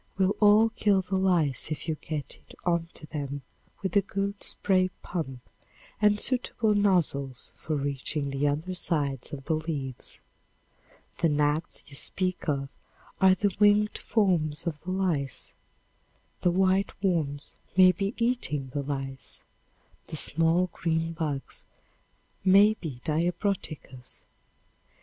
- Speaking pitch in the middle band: Yes, medium, 165 Hz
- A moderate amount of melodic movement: Yes, average, 4.9 semitones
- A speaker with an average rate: No, slow, 130 wpm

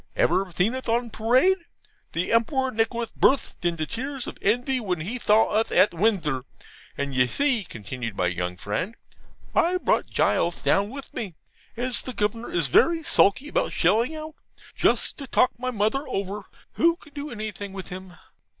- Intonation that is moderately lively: No, wide, 6.3 semitones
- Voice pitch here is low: No, high, 220 Hz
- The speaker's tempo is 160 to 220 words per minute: Yes, average, 170 wpm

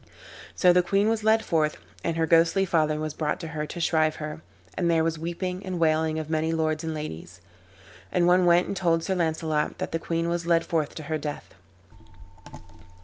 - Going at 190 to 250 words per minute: Yes, average, 200 wpm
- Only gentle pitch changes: Yes, narrow, 1.9 semitones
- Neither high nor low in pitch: Yes, medium, 165 Hz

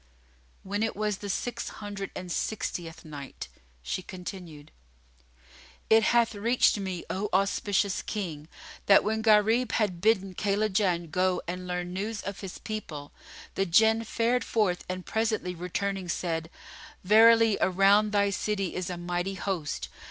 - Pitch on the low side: No, high, 195 Hz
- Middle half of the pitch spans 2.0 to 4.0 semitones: Yes, average, 3.1 semitones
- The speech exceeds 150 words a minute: No, average, 140 wpm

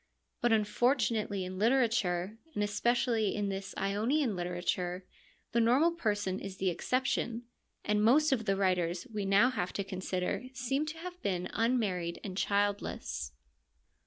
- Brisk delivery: No, average, 140 wpm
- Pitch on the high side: Yes, high, 205 Hz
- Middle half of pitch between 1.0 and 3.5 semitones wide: No, average, 4.2 semitones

